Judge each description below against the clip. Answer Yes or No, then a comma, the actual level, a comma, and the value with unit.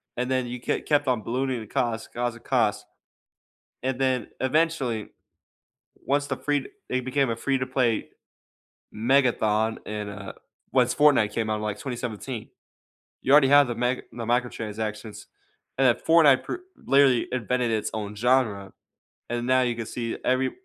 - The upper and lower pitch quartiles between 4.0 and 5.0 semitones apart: No, average, 2.9 semitones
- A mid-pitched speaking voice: No, low, 125 Hz